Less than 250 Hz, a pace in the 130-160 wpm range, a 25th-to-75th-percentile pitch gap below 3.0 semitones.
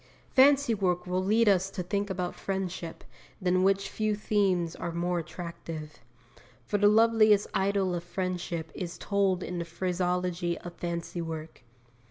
Yes: medium, 185 Hz; average, 150 wpm; narrow, 2.5 semitones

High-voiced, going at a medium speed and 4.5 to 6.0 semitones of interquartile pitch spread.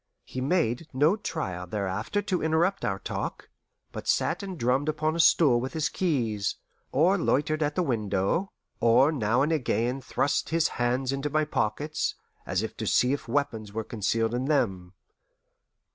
No: low, 135 Hz; average, 165 wpm; wide, 5.6 semitones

